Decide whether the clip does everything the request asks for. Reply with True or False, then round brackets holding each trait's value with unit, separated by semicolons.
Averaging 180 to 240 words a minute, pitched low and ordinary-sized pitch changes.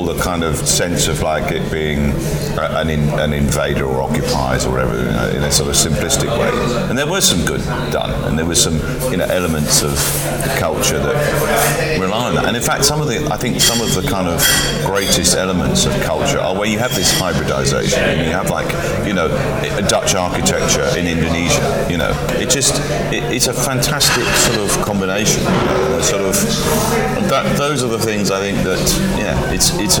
True (205 wpm; 75 Hz; 4.6 semitones)